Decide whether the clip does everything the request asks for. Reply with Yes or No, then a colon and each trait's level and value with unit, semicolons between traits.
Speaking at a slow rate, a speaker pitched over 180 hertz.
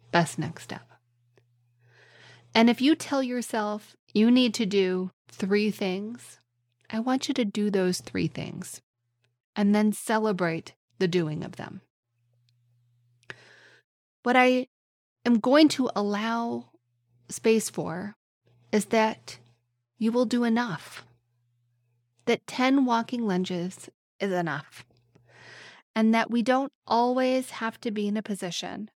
Yes: slow, 120 wpm; high, 190 Hz